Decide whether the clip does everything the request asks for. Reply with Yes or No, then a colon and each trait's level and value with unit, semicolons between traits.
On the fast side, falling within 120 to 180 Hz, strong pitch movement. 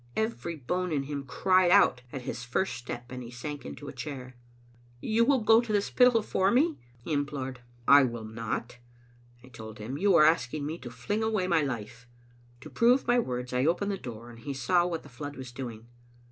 Yes: fast, 215 wpm; medium, 140 Hz; wide, 7.2 semitones